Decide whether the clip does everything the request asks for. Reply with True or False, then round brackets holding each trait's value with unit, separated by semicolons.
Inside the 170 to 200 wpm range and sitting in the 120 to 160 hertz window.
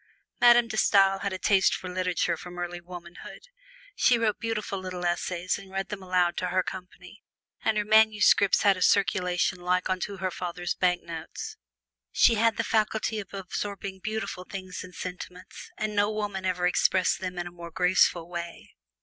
False (175 wpm; 185 Hz)